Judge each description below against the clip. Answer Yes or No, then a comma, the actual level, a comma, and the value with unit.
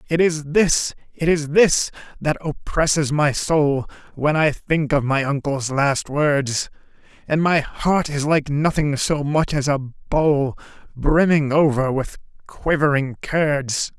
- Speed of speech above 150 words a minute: No, average, 145 wpm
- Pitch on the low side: No, medium, 145 Hz